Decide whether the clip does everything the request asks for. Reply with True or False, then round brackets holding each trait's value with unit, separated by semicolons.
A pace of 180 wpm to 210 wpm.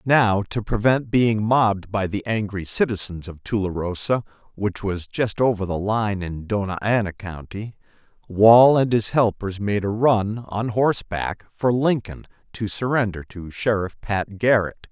False (155 wpm)